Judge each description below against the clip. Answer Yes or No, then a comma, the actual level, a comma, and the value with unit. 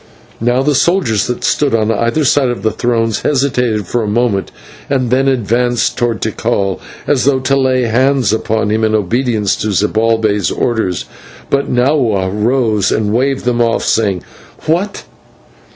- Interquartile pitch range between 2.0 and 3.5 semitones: Yes, average, 3.2 semitones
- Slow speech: No, average, 155 wpm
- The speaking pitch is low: Yes, low, 120 Hz